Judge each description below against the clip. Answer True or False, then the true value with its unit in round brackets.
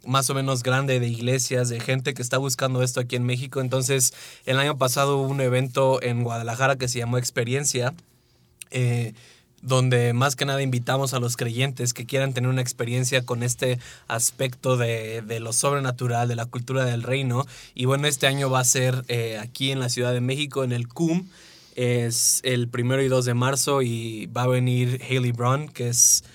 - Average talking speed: False (195 wpm)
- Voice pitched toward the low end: True (125 Hz)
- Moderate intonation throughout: False (1.6 semitones)